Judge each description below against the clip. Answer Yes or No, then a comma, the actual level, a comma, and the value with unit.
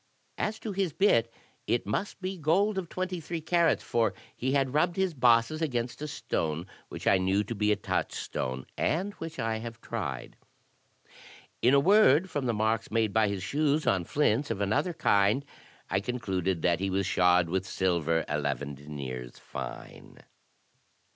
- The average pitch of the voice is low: Yes, low, 115 Hz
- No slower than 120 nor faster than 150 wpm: No, average, 165 wpm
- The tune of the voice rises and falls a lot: Yes, wide, 8.7 semitones